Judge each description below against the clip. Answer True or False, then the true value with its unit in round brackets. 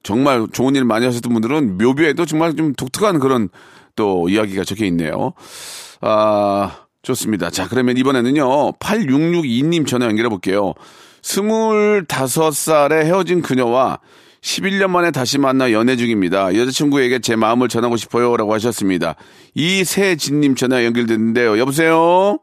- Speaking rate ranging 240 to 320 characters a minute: True (315 characters per minute)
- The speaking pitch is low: True (130 Hz)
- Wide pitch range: True (5.8 semitones)